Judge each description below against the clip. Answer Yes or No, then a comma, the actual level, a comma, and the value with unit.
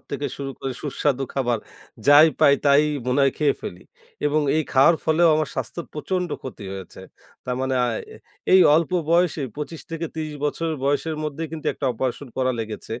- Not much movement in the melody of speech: No, average, 3.2 semitones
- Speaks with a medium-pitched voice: Yes, medium, 145 Hz